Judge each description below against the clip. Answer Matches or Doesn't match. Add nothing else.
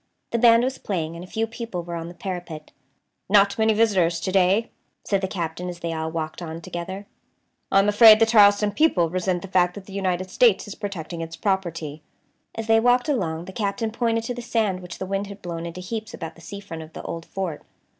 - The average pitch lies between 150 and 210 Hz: Matches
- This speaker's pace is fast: Matches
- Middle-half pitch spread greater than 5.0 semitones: Doesn't match